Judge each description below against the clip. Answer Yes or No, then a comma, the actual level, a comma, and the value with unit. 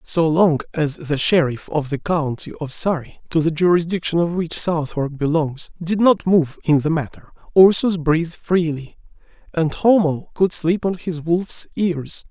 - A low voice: No, medium, 165 Hz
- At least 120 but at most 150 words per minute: No, average, 165 wpm